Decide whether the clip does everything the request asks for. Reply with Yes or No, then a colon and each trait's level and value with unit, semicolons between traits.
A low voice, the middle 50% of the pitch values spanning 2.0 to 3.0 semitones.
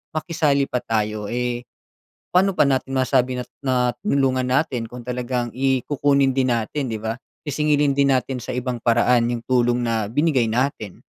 Yes: low, 125 Hz; narrow, 2.6 semitones